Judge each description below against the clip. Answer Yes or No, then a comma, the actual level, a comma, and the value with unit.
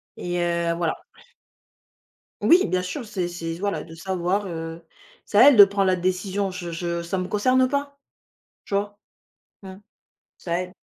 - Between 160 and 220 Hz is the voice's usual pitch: Yes, medium, 185 Hz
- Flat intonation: No, average, 3.0 semitones